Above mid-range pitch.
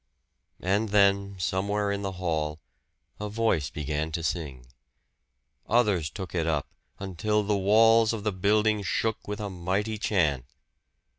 No: low, 100 Hz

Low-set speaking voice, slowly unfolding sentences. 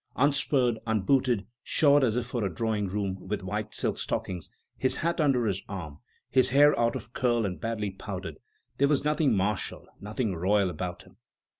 No: low, 110 Hz; average, 175 wpm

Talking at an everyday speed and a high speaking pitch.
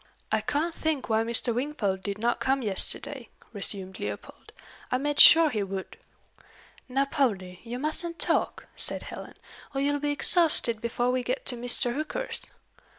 Yes: average, 155 wpm; very high, 250 Hz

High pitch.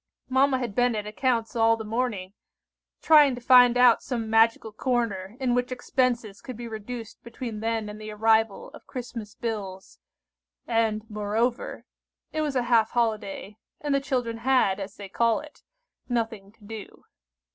Yes: high, 230 Hz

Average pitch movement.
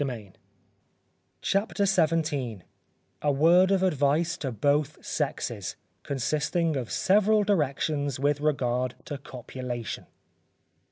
Yes: average, 4.6 semitones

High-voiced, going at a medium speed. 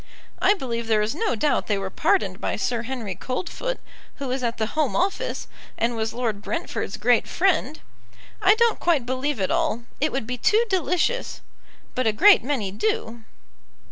Yes: very high, 250 Hz; average, 175 wpm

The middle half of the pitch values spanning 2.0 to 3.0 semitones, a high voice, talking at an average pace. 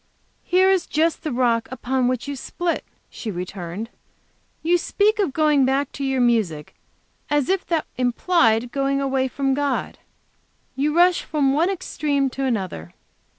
No: average, 4.4 semitones; very high, 275 Hz; average, 150 wpm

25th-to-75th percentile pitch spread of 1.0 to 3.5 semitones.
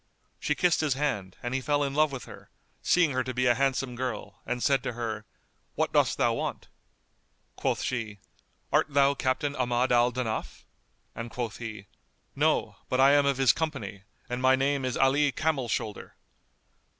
Yes: narrow, 2.6 semitones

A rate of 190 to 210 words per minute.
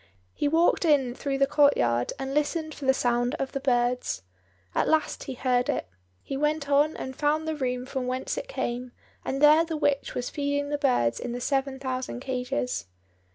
Yes: average, 195 wpm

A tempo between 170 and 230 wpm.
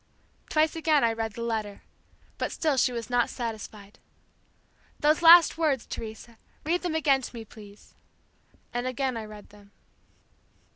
No: average, 150 wpm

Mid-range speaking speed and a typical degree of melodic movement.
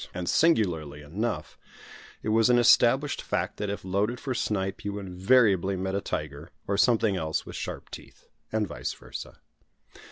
Yes: average, 160 wpm; average, 3.8 semitones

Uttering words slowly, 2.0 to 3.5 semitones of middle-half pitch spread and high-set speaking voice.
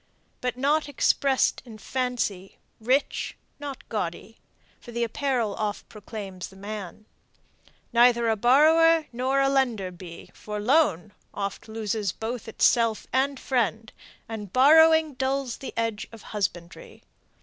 No: slow, 125 wpm; average, 4.3 semitones; high, 235 Hz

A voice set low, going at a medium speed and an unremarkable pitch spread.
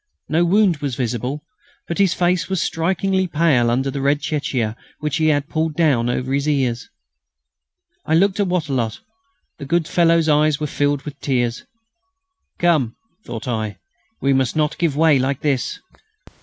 No: medium, 150 Hz; average, 160 wpm; average, 4.0 semitones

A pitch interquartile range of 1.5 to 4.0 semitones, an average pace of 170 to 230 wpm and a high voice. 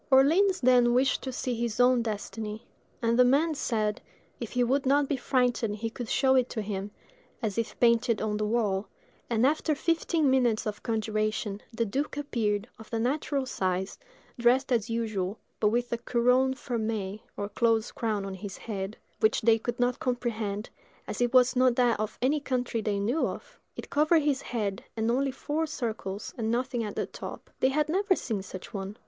Yes: average, 3.5 semitones; average, 190 wpm; high, 235 Hz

